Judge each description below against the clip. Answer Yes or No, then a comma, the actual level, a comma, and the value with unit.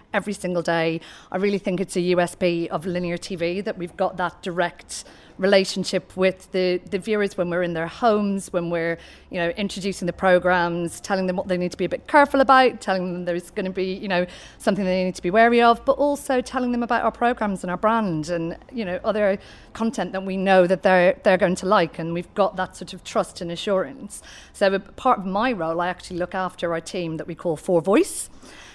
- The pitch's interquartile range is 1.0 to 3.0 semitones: Yes, narrow, 2.6 semitones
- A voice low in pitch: No, medium, 185 Hz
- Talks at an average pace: No, fast, 230 wpm